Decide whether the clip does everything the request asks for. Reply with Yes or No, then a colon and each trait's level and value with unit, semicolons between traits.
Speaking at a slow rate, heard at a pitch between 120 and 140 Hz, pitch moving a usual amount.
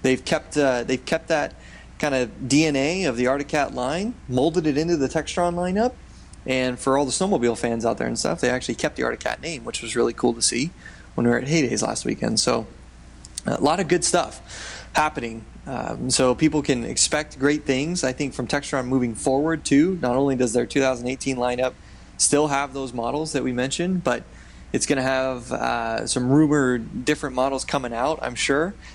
No: average, 200 wpm; low, 135 Hz; average, 3.3 semitones